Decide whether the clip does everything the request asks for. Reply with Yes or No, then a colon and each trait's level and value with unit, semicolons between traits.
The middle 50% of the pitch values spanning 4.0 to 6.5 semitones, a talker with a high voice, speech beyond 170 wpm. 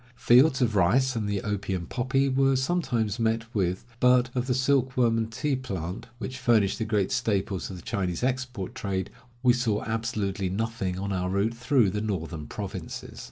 No: average, 4.4 semitones; low, 115 Hz; average, 180 wpm